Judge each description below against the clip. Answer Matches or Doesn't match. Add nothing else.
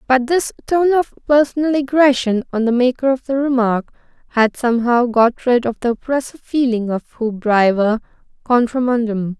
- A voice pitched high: Matches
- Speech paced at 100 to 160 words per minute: Matches